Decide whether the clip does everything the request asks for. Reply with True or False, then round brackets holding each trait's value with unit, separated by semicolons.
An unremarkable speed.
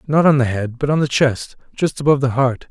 False (265 wpm)